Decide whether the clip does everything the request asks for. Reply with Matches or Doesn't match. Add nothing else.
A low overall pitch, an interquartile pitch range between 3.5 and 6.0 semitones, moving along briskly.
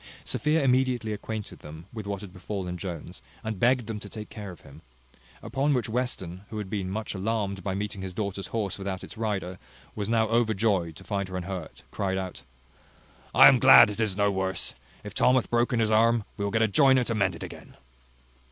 Doesn't match